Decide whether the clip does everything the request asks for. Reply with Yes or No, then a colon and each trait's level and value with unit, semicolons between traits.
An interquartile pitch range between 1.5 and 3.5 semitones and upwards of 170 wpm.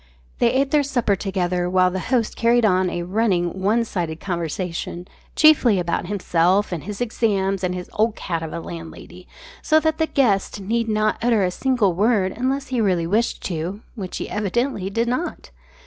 No: average, 4.6 semitones; average, 180 wpm